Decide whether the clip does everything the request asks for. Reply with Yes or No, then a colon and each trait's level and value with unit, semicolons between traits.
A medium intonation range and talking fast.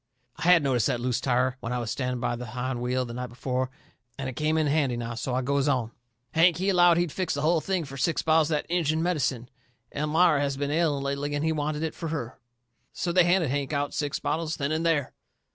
Yes: average, 4.1 semitones; fast, 245 wpm